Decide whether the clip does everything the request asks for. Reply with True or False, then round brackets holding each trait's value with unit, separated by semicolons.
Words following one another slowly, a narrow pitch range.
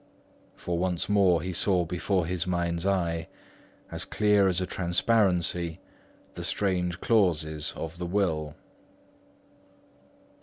True (110 wpm; 2.2 semitones)